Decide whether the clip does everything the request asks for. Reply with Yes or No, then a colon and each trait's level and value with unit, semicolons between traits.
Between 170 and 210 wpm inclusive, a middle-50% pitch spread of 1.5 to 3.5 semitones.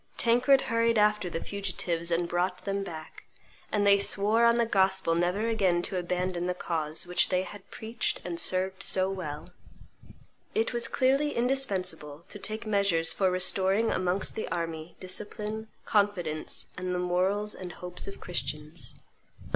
No: average, 155 wpm; average, 3.2 semitones